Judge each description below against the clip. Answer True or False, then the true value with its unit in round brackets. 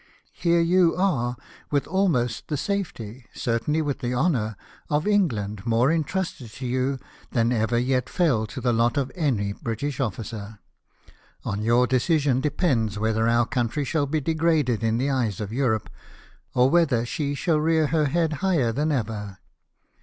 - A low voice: True (130 Hz)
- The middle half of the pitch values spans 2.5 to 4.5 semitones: False (5.3 semitones)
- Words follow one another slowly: False (165 wpm)